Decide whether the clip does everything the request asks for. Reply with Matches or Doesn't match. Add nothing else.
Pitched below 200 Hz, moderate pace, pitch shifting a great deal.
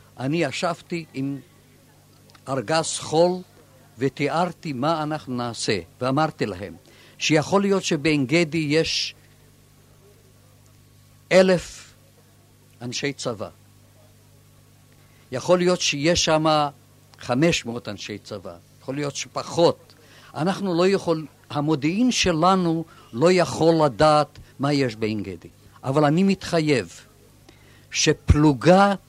Doesn't match